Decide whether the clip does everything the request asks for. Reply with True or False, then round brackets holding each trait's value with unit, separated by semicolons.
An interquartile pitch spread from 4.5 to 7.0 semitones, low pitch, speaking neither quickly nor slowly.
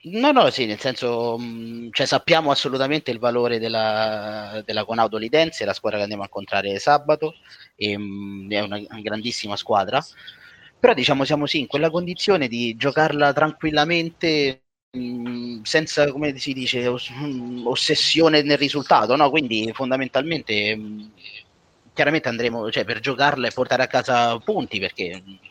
True (5.0 semitones; 125 Hz; 150 wpm)